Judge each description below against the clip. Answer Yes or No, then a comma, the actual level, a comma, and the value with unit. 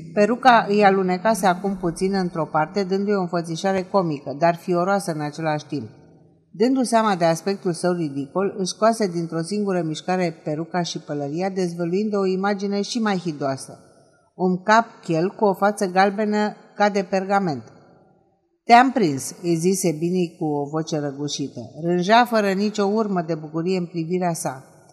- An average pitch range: Yes, average, 3.6 semitones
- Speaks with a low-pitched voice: No, medium, 180 Hz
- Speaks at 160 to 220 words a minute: No, average, 150 wpm